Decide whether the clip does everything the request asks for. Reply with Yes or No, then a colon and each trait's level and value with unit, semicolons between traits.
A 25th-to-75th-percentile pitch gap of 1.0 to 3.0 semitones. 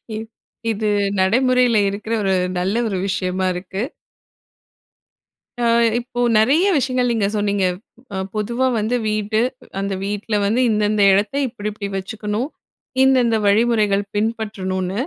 Yes: average, 2.7 semitones